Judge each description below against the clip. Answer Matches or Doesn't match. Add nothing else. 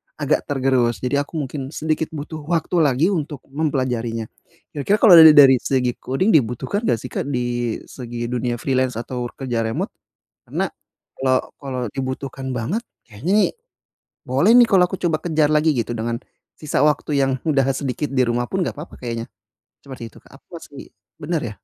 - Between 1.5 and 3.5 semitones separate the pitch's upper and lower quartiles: Doesn't match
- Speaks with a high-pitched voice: Doesn't match